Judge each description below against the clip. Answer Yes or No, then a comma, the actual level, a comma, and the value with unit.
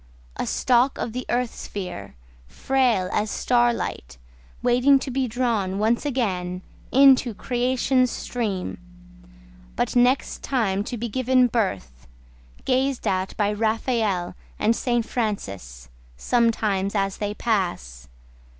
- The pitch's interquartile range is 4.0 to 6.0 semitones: Yes, average, 4.6 semitones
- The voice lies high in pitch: Yes, high, 225 Hz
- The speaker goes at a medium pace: No, slow, 120 wpm